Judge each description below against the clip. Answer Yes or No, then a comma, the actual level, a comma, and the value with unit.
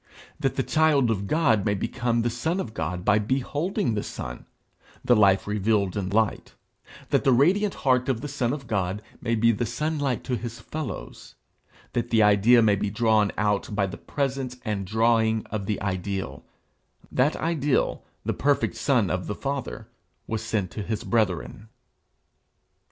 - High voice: No, low, 110 Hz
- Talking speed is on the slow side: No, average, 170 wpm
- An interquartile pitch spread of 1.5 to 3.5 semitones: No, average, 4.1 semitones